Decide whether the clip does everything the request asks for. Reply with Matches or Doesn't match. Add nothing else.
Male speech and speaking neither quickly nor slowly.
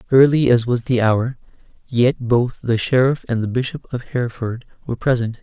Matches